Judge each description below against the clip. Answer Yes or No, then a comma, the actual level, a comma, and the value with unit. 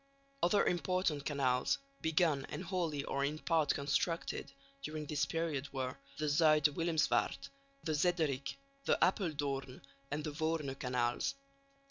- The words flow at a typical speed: No, slow, 125 wpm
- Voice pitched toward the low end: No, medium, 150 Hz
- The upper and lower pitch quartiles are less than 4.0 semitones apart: Yes, average, 2.9 semitones